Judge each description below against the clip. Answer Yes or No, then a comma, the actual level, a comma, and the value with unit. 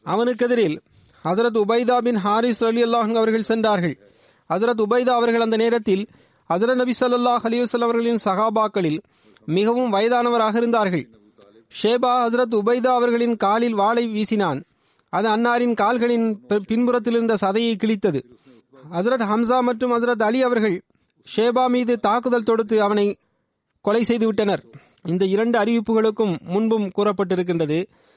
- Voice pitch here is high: Yes, high, 225 Hz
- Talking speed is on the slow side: No, average, 115 wpm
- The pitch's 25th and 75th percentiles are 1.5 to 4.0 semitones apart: Yes, average, 2.8 semitones